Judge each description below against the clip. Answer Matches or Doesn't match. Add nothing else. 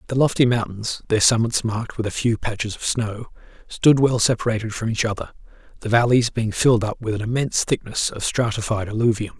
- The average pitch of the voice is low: Matches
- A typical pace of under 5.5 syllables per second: Doesn't match